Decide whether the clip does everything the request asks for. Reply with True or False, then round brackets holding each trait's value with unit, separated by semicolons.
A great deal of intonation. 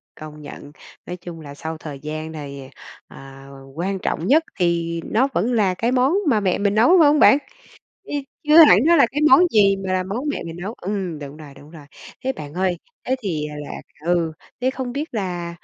True (7.6 semitones)